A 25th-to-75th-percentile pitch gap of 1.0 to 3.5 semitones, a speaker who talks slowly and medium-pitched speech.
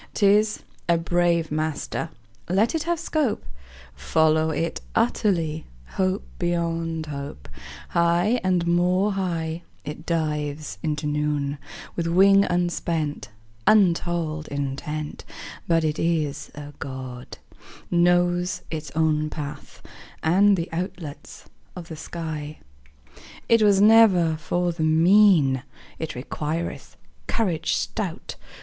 Yes: average, 2.9 semitones; slow, 110 wpm; medium, 165 Hz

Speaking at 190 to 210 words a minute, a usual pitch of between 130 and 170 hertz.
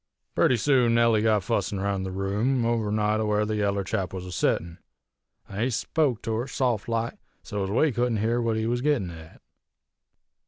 No: fast, 205 wpm; low, 110 Hz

